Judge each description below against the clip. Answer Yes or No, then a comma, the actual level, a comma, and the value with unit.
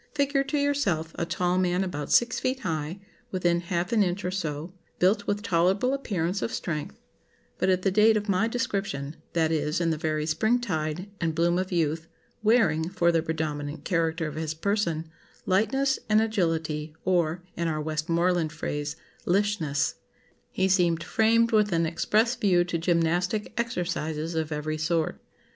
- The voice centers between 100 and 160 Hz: No, medium, 175 Hz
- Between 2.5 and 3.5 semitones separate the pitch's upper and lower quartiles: No, average, 4.3 semitones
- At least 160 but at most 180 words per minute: Yes, average, 165 wpm